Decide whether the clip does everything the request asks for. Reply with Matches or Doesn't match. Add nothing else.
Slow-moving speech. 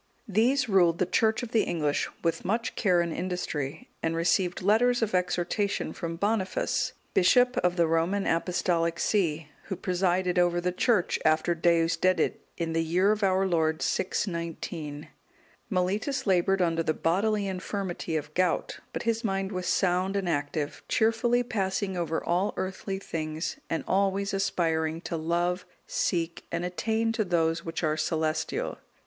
Doesn't match